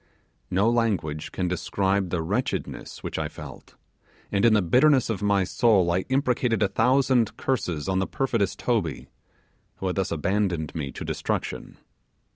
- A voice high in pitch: No, low, 100 Hz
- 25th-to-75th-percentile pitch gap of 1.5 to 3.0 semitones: No, average, 4.6 semitones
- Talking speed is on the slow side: No, average, 155 wpm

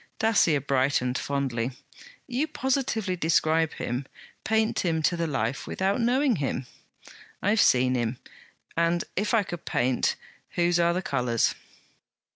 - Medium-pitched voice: Yes, medium, 165 Hz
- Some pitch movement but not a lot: No, wide, 7.6 semitones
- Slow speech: Yes, slow, 130 wpm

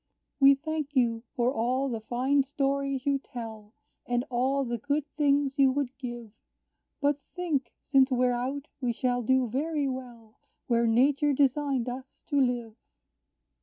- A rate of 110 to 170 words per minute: Yes, average, 150 wpm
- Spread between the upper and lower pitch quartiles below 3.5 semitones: Yes, narrow, 2.6 semitones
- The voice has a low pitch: No, very high, 260 Hz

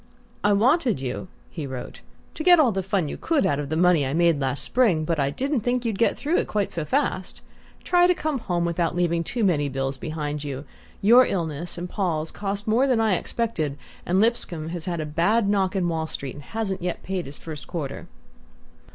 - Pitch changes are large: Yes, wide, 6.4 semitones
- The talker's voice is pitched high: No, medium, 175 Hz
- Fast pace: Yes, fast, 215 wpm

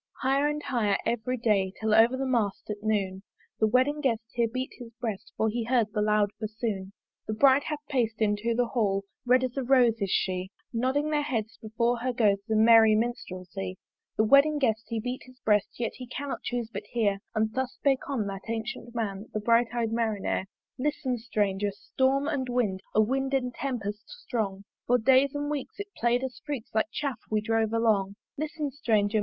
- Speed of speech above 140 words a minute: Yes, average, 195 wpm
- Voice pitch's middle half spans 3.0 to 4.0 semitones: Yes, average, 3.4 semitones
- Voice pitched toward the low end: No, high, 230 Hz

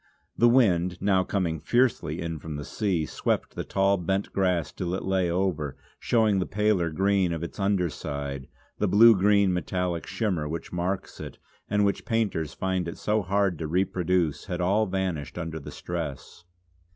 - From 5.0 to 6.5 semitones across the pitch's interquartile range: No, average, 3.1 semitones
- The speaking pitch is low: Yes, very low, 90 Hz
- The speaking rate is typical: Yes, average, 175 wpm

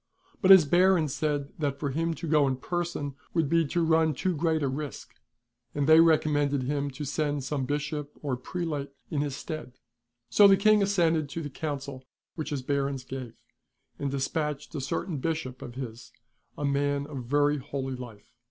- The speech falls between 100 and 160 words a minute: No, average, 180 wpm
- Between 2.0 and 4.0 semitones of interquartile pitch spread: Yes, narrow, 2.6 semitones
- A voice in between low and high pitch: Yes, medium, 145 Hz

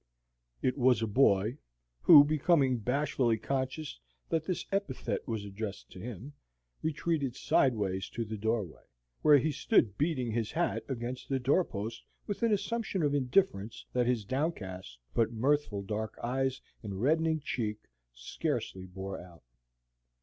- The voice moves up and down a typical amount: No, wide, 5.7 semitones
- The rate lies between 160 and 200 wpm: No, average, 140 wpm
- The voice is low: Yes, low, 125 Hz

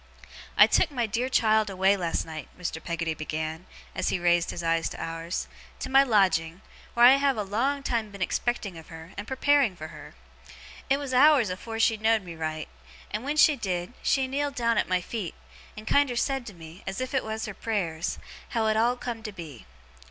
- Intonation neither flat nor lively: No, wide, 6.4 semitones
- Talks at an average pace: No, fast, 210 wpm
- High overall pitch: Yes, high, 215 Hz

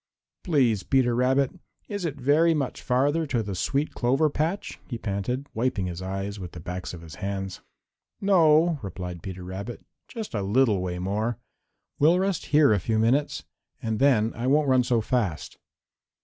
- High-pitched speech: No, low, 120 Hz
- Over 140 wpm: Yes, average, 170 wpm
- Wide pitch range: Yes, wide, 6.7 semitones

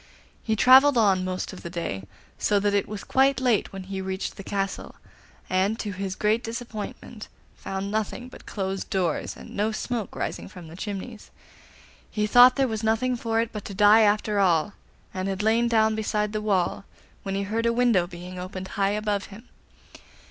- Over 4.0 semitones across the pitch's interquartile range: No, average, 2.7 semitones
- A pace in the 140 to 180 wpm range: No, average, 190 wpm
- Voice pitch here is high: Yes, high, 210 Hz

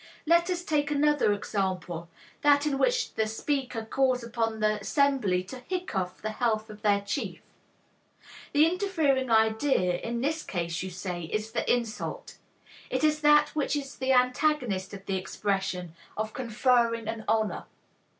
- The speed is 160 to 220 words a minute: No, average, 150 wpm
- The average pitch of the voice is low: No, high, 230 Hz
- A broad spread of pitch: Yes, wide, 6.0 semitones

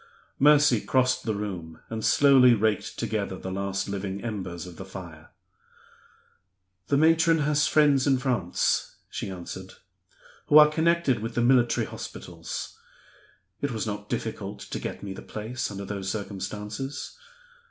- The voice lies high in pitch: No, low, 110 Hz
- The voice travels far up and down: Yes, wide, 5.8 semitones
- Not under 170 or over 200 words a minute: No, average, 140 wpm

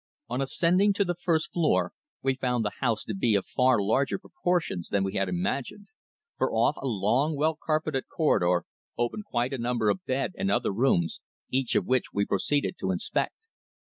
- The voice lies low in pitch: Yes, low, 130 Hz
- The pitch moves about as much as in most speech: No, wide, 6.8 semitones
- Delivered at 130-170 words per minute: No, average, 185 wpm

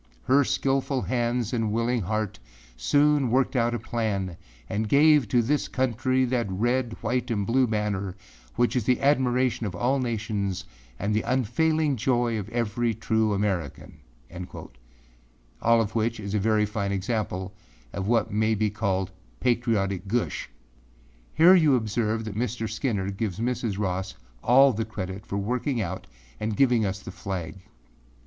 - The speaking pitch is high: No, low, 110 Hz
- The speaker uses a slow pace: No, average, 155 wpm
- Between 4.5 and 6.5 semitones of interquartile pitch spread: No, average, 3.7 semitones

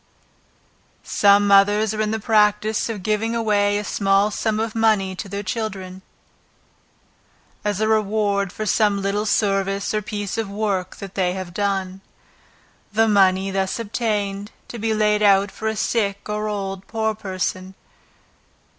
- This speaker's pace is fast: No, average, 145 wpm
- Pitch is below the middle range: No, high, 205 Hz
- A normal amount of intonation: No, narrow, 1.6 semitones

